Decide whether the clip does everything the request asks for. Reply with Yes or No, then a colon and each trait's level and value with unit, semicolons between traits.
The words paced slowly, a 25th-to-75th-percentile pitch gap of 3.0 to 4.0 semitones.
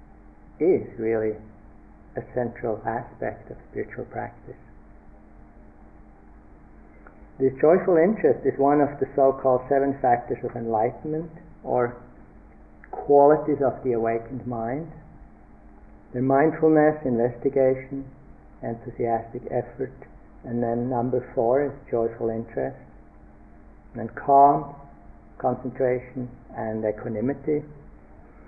No: slow, 95 wpm; average, 4.6 semitones